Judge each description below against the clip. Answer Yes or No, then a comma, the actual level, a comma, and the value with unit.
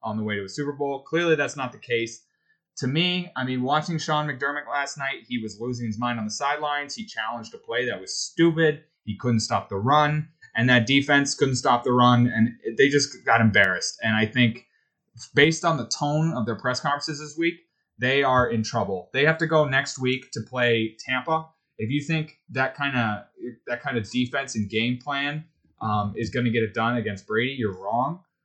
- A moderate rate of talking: No, fast, 215 wpm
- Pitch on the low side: Yes, low, 130 Hz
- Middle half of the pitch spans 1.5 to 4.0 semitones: No, average, 4.6 semitones